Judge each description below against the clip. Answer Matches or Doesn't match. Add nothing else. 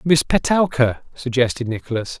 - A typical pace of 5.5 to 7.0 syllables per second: Doesn't match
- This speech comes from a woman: Doesn't match